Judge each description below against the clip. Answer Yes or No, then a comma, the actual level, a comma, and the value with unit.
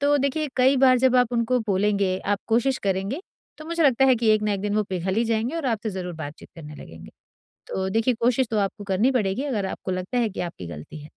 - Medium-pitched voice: No, high, 220 Hz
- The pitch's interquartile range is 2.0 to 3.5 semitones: No, average, 5.1 semitones